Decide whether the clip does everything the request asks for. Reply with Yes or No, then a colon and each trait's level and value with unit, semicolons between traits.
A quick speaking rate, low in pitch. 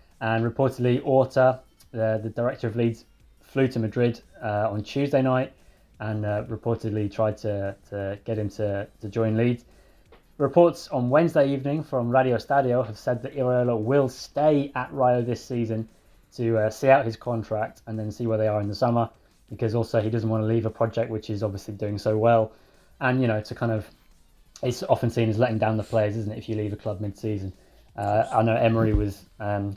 Yes: fast, 210 wpm; low, 115 Hz